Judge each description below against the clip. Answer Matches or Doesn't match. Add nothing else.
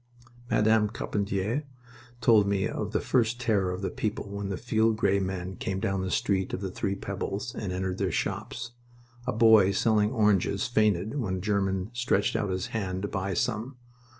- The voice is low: Matches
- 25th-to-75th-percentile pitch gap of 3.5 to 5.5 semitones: Doesn't match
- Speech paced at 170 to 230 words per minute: Matches